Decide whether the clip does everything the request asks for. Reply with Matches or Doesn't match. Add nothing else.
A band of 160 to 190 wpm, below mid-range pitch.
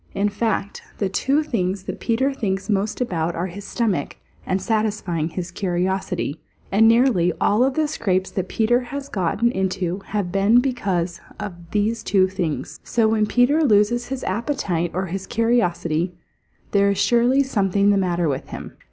Doesn't match